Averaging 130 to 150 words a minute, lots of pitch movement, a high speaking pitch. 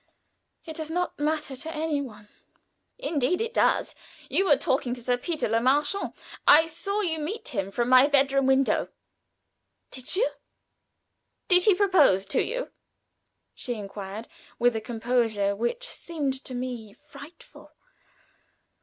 Yes: average, 140 wpm; wide, 5.7 semitones; very high, 275 Hz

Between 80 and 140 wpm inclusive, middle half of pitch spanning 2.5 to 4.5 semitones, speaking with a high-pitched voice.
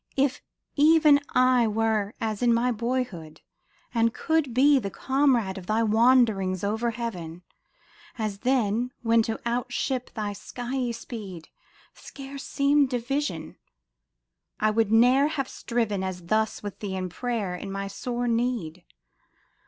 Yes: slow, 135 wpm; average, 3.8 semitones; high, 230 Hz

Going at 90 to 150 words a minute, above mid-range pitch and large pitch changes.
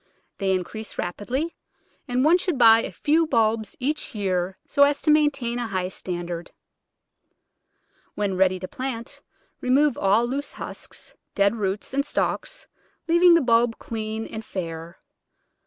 Yes: average, 140 wpm; high, 230 Hz; wide, 6.4 semitones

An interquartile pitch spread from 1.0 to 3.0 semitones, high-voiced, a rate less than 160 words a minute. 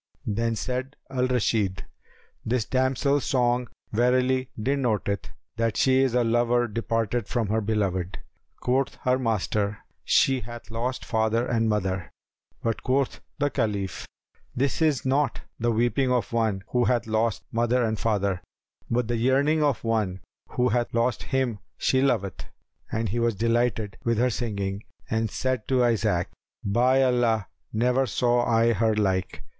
No: narrow, 2.6 semitones; low, 115 Hz; average, 150 wpm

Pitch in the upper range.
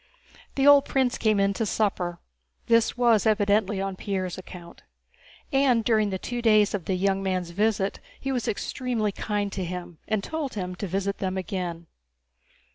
Yes: high, 200 Hz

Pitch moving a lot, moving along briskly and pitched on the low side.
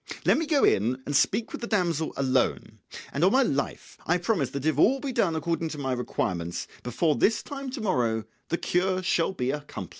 No: wide, 7.6 semitones; fast, 210 wpm; medium, 165 Hz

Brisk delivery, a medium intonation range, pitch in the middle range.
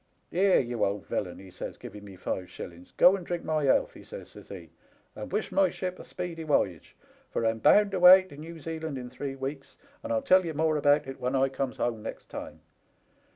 No: fast, 230 wpm; wide, 6.6 semitones; medium, 145 Hz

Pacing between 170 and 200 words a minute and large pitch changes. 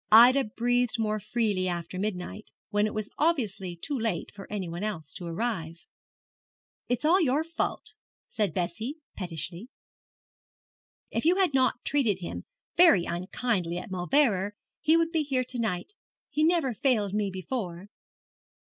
No: average, 145 wpm; wide, 6.0 semitones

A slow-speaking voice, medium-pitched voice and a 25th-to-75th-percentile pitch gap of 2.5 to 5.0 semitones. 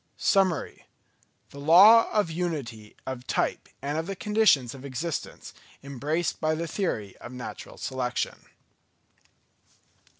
No: slow, 120 wpm; medium, 155 Hz; wide, 5.5 semitones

